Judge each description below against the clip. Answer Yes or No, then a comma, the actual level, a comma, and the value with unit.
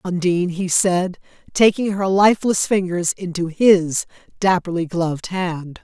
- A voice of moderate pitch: Yes, medium, 180 Hz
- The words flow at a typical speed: No, slow, 125 wpm